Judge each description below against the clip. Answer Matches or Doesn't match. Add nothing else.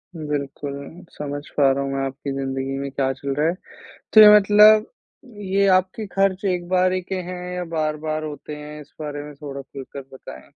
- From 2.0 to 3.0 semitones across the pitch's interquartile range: Doesn't match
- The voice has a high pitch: Doesn't match